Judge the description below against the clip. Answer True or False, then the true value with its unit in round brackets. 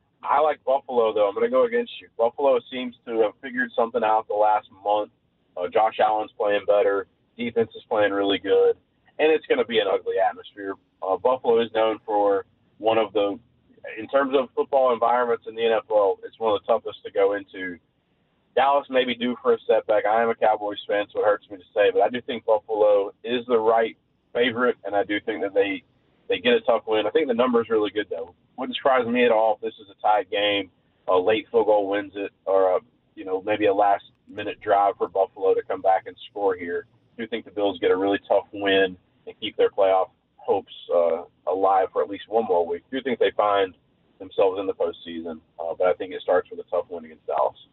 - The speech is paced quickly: True (235 wpm)